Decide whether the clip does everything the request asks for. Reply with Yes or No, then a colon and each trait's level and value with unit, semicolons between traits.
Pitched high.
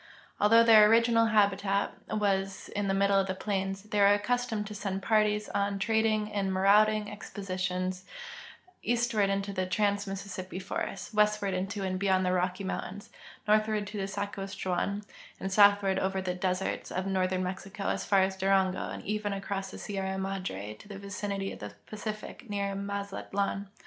Yes: high, 200 Hz